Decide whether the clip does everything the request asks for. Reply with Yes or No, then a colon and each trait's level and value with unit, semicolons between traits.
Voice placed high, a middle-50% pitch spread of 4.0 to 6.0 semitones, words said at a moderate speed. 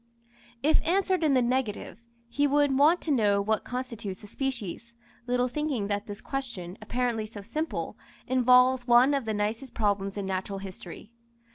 Yes: high, 240 Hz; average, 4.6 semitones; average, 160 wpm